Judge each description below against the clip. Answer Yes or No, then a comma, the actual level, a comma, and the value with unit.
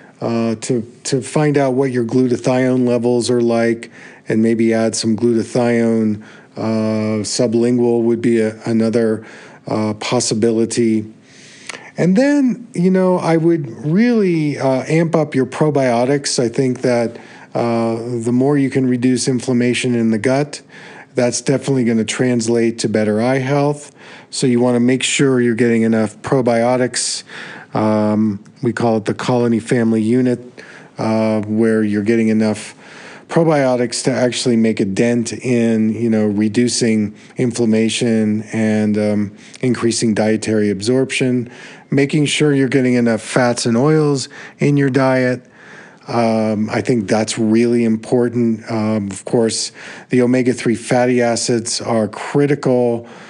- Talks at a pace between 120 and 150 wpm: Yes, average, 140 wpm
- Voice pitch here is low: Yes, low, 120 Hz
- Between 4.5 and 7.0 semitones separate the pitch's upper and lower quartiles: No, narrow, 2.5 semitones